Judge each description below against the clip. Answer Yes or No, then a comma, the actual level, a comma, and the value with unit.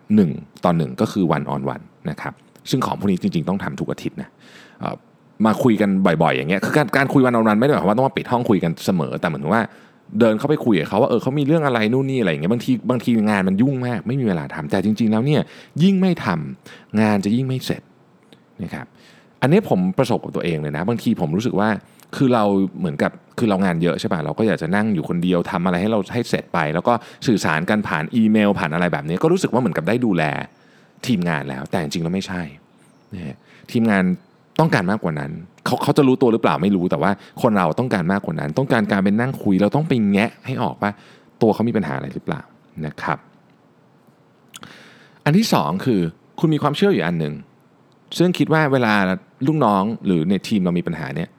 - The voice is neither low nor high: No, low, 110 Hz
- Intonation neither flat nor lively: No, wide, 7.3 semitones